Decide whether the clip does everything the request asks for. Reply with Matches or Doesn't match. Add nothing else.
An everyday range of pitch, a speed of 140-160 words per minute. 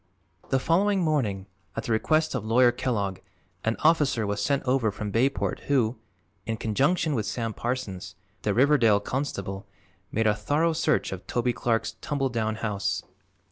Matches